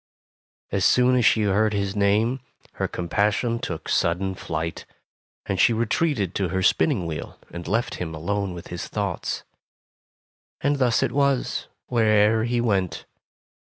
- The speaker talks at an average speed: Yes, average, 155 wpm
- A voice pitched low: Yes, low, 105 Hz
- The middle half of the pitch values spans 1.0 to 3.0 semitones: No, average, 4.0 semitones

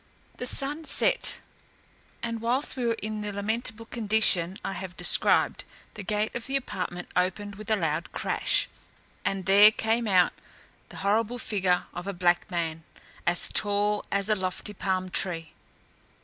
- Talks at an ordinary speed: Yes, average, 155 wpm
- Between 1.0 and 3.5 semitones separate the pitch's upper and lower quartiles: Yes, average, 3.2 semitones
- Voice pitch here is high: Yes, high, 205 Hz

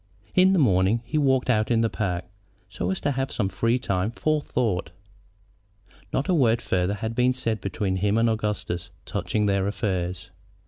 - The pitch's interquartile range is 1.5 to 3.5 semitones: No, average, 4.9 semitones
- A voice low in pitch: Yes, low, 110 Hz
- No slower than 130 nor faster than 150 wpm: No, average, 175 wpm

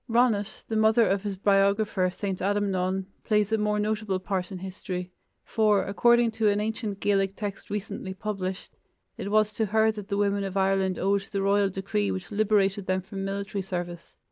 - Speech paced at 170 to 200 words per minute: Yes, average, 180 wpm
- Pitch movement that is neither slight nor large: No, narrow, 1.8 semitones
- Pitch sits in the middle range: No, high, 200 Hz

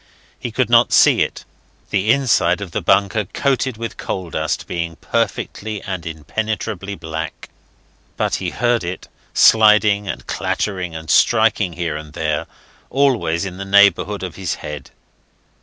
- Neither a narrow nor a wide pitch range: Yes, average, 4.5 semitones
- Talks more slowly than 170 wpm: Yes, average, 145 wpm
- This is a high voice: No, very low, 95 Hz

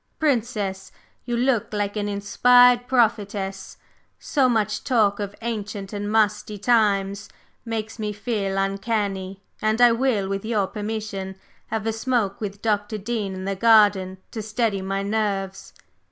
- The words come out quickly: No, average, 140 wpm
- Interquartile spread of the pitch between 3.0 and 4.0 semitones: No, narrow, 2.4 semitones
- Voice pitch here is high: Yes, high, 210 Hz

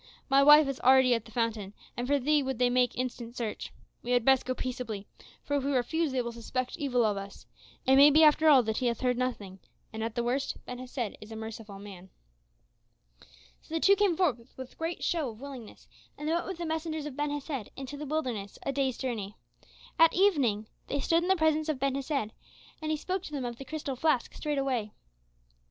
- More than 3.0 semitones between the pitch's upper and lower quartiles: Yes, average, 4.2 semitones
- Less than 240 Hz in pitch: No, very high, 260 Hz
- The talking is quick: Yes, fast, 220 wpm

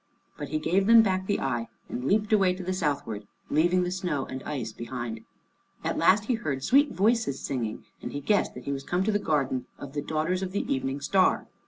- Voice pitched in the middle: Yes, medium, 160 Hz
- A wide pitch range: Yes, wide, 6.1 semitones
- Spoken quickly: Yes, fast, 220 wpm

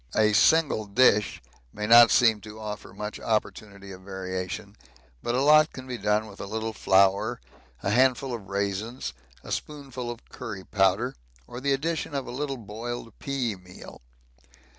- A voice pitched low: Yes, low, 110 Hz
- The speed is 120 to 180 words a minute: Yes, average, 160 wpm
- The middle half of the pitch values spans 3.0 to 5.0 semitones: Yes, average, 4.2 semitones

